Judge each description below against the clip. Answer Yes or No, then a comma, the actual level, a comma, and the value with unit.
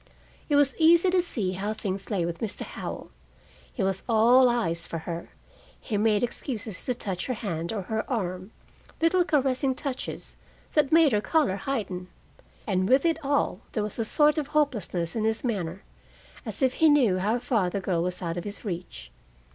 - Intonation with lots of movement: Yes, wide, 6.6 semitones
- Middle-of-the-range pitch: No, high, 220 Hz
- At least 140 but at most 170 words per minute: No, average, 185 wpm